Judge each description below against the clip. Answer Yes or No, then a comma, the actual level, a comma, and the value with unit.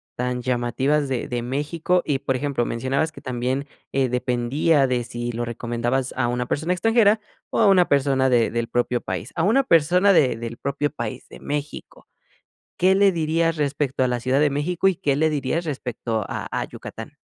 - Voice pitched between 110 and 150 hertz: Yes, low, 135 Hz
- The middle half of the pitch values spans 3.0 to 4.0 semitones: No, average, 4.5 semitones